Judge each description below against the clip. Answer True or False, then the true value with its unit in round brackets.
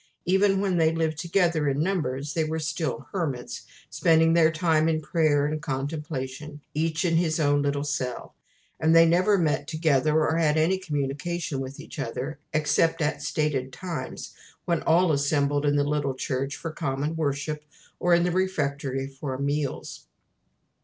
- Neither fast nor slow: True (160 wpm)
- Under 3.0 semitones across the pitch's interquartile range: True (2.6 semitones)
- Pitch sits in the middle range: True (155 Hz)